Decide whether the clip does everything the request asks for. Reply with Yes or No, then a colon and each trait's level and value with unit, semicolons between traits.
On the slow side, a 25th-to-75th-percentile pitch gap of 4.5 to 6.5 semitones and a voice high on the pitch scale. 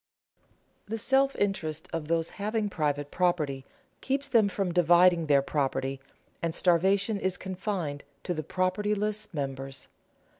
No: slow, 125 wpm; average, 5.1 semitones; medium, 180 Hz